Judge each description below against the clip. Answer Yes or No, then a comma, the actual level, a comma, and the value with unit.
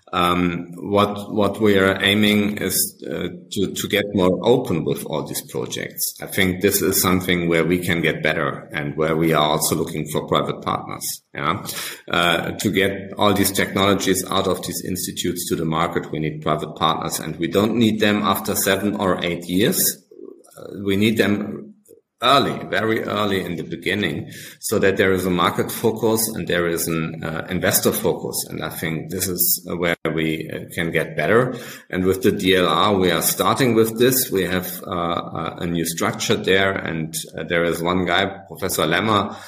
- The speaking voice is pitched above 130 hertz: No, very low, 95 Hz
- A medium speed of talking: Yes, average, 190 wpm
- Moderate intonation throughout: Yes, average, 3.3 semitones